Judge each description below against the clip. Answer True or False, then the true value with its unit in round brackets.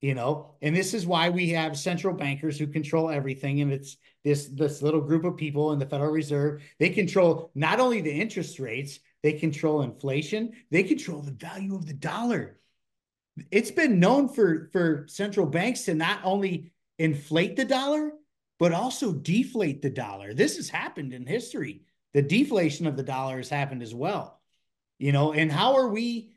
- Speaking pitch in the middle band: True (160 Hz)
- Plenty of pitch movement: False (5.0 semitones)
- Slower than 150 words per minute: False (180 wpm)